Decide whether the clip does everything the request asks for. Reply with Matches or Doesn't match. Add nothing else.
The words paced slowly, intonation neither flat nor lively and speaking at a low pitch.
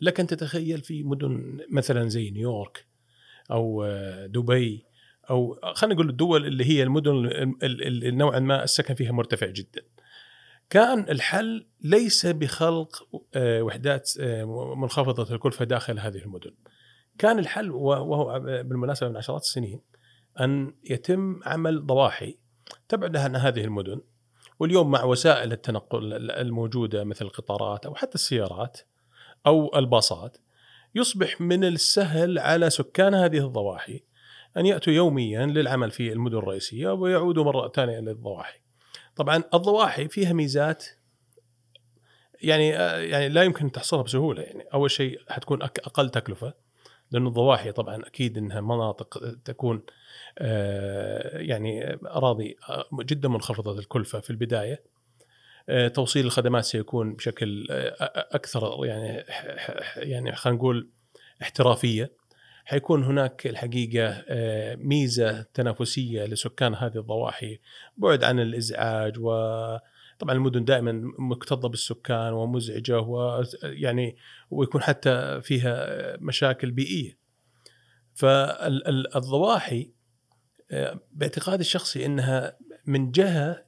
Doesn't match